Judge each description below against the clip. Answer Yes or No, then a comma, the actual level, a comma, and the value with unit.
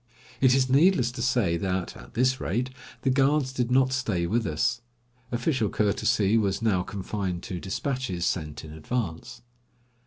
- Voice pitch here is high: No, low, 115 Hz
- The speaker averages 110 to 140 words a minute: No, average, 155 wpm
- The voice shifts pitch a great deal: Yes, wide, 5.7 semitones